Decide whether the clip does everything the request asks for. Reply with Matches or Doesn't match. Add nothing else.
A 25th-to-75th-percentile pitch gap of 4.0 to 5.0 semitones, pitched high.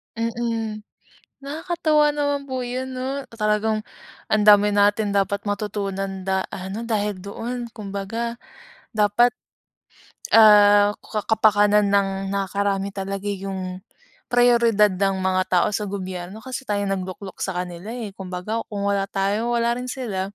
Doesn't match